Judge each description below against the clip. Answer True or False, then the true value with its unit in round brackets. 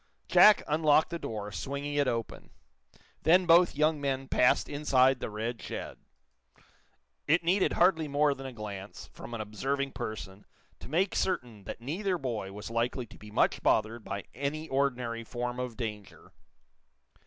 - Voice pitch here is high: False (130 Hz)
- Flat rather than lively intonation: False (5.1 semitones)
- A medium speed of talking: True (155 wpm)